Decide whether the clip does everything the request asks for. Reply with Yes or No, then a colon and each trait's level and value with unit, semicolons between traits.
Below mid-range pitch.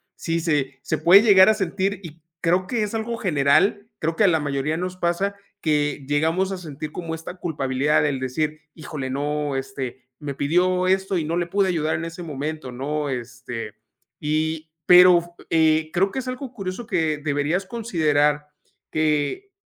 No: medium, 160 Hz